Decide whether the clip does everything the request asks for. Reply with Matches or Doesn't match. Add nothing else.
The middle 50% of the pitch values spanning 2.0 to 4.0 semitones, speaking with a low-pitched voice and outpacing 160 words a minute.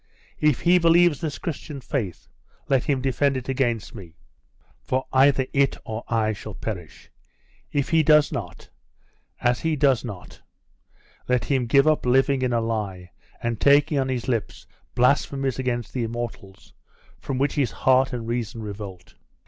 Doesn't match